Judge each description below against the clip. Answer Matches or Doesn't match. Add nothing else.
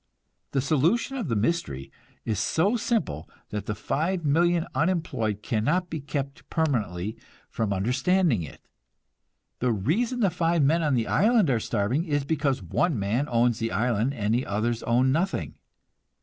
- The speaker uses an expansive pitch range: Matches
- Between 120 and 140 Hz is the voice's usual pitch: Matches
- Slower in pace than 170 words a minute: Matches